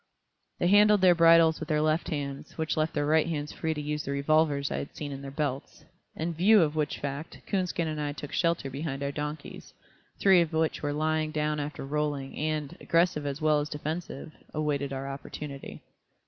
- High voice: No, medium, 150 Hz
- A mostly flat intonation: Yes, narrow, 1.9 semitones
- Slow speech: No, average, 200 wpm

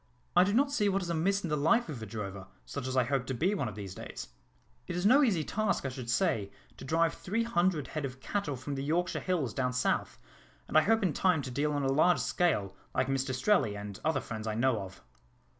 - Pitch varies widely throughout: Yes, wide, 6.3 semitones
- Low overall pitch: No, medium, 145 Hz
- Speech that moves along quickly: Yes, fast, 245 wpm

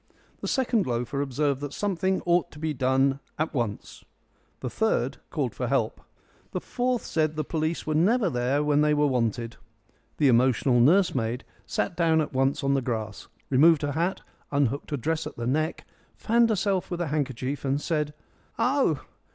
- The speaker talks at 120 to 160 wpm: No, average, 175 wpm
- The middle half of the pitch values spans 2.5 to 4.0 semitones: No, average, 4.4 semitones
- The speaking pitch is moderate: Yes, medium, 150 Hz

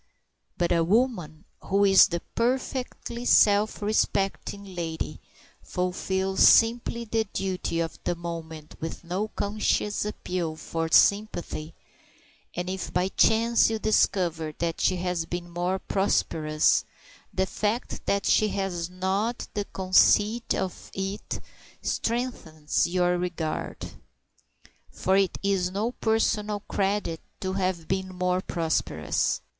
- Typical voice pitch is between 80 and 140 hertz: No, high, 190 Hz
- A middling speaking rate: No, slow, 120 wpm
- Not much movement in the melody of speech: No, average, 3.3 semitones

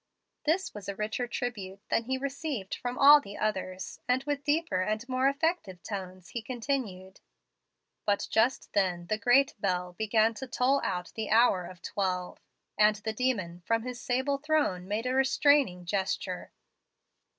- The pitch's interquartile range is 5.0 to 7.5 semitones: Yes, wide, 5.6 semitones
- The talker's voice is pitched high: Yes, high, 220 Hz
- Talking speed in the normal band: Yes, average, 160 wpm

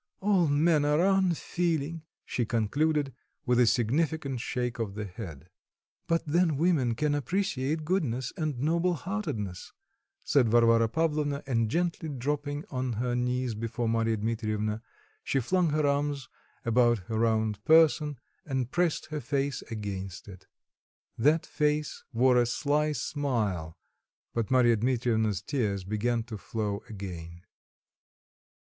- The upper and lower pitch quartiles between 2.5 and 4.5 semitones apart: No, average, 5.1 semitones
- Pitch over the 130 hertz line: No, low, 125 Hz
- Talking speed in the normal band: No, slow, 130 wpm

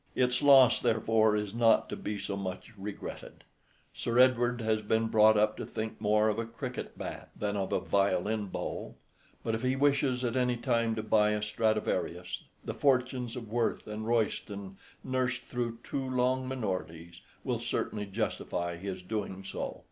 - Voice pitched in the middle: No, low, 110 Hz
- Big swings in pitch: No, average, 3.1 semitones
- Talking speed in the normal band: Yes, average, 170 wpm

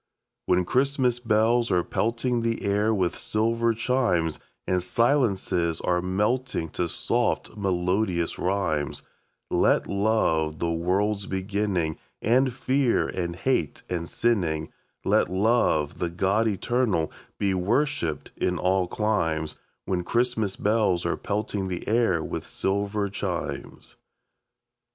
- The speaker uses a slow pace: Yes, slow, 120 wpm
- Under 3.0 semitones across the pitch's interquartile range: No, average, 4.6 semitones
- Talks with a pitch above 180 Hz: No, low, 100 Hz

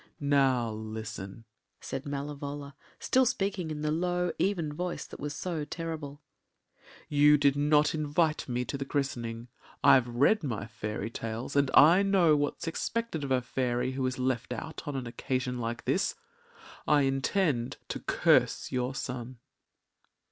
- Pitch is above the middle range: No, medium, 140 Hz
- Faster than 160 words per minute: No, average, 150 wpm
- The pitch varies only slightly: No, average, 3.6 semitones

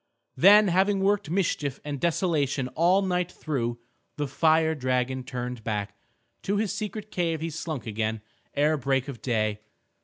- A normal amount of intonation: No, wide, 6.1 semitones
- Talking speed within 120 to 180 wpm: Yes, average, 150 wpm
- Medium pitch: Yes, medium, 150 Hz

